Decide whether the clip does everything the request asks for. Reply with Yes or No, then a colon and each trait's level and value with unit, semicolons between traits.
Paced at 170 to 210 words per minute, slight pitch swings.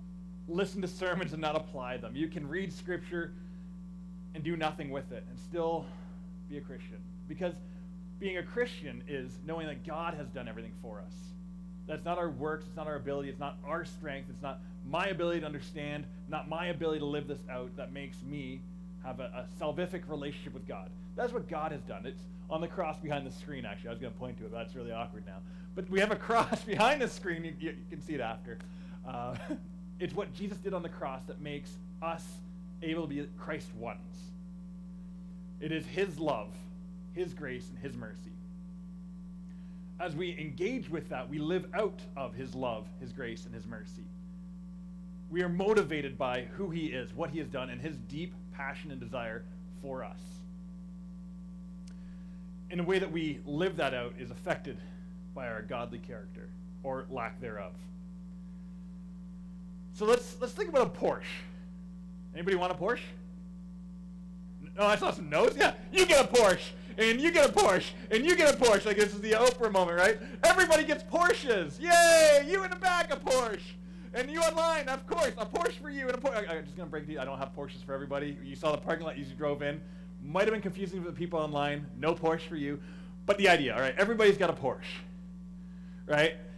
Yes: average, 200 wpm; narrow, 1.7 semitones